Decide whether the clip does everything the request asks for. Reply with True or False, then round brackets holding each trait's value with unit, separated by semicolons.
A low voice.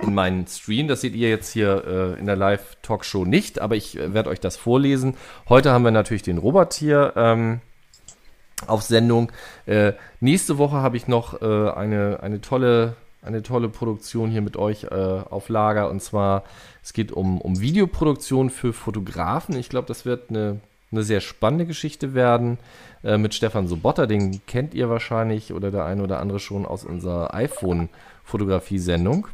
True (110 Hz)